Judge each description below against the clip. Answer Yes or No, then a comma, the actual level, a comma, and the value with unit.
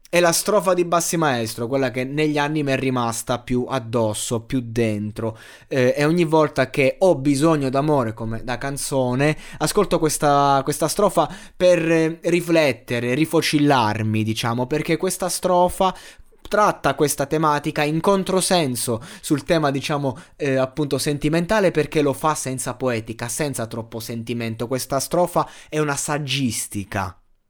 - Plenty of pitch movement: No, average, 4.7 semitones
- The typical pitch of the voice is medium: Yes, medium, 145 Hz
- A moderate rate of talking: Yes, average, 135 wpm